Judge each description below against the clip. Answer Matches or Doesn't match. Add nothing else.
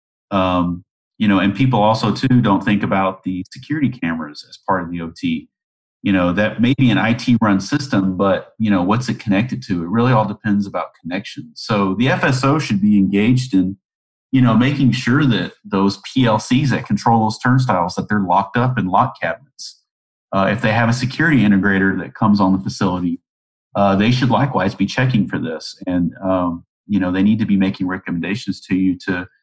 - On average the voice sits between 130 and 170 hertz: Doesn't match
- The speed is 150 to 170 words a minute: Doesn't match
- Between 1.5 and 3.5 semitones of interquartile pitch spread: Doesn't match